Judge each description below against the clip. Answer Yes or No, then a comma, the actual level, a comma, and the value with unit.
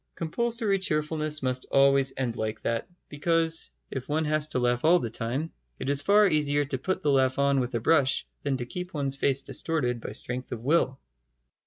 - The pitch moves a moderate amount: Yes, average, 3.7 semitones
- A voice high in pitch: No, medium, 140 Hz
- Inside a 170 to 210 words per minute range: Yes, average, 195 wpm